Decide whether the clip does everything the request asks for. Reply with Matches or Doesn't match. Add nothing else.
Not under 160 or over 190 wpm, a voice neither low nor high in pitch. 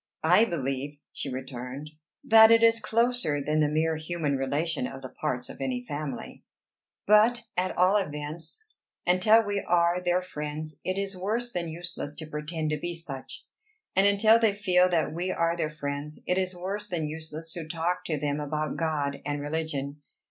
Matches